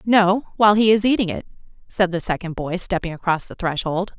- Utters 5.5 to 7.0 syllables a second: Yes, 5.7 syllables/s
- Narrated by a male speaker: No, female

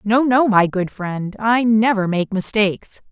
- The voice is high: Yes, high, 210 Hz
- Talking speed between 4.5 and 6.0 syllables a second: No, 4.1 syllables/s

